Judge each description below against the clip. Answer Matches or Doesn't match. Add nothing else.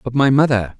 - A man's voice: Matches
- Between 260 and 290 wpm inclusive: Doesn't match